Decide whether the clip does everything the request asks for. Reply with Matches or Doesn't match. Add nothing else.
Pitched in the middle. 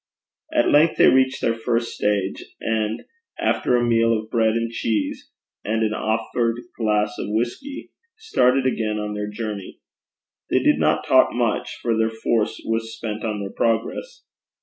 Doesn't match